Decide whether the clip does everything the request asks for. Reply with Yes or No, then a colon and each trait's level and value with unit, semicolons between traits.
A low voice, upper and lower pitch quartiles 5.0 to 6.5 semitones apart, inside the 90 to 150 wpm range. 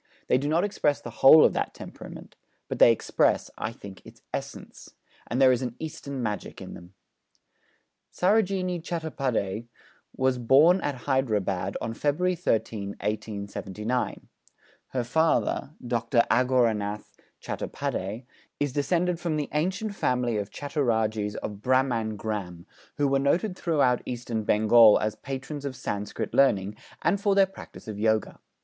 Yes: low, 125 Hz; wide, 5.6 semitones; average, 140 wpm